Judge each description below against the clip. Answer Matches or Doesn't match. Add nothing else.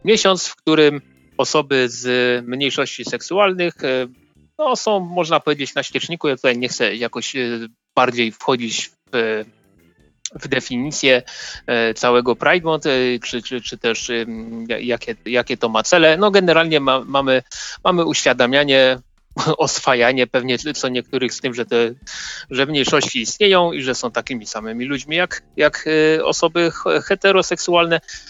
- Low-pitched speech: Matches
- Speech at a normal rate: Matches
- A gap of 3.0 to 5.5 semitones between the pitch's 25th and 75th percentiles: Matches